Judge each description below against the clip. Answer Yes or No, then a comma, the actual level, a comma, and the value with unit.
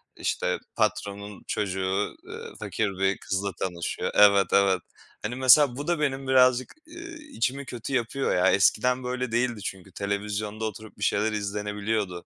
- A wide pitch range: No, average, 4.3 semitones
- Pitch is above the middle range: No, low, 105 Hz